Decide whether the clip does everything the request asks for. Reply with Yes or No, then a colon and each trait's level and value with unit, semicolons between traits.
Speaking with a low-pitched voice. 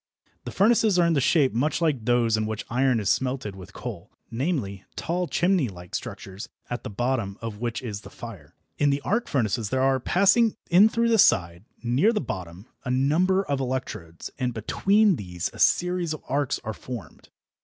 Yes: low, 130 Hz